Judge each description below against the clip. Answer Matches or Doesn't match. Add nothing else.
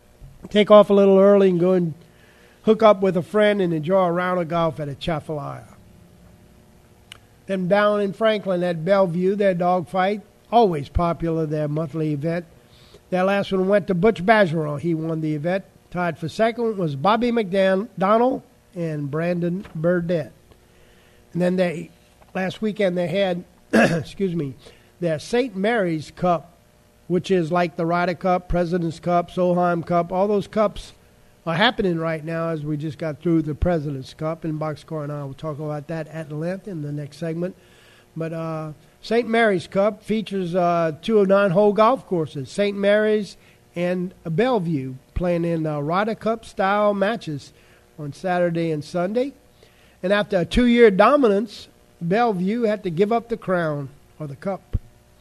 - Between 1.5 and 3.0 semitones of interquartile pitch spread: Doesn't match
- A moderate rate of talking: Matches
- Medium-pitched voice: Matches